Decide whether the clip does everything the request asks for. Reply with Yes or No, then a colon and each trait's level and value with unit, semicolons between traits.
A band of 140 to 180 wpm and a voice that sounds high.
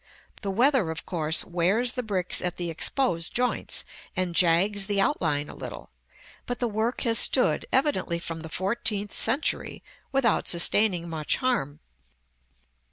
Yes: average, 145 wpm; high, 195 Hz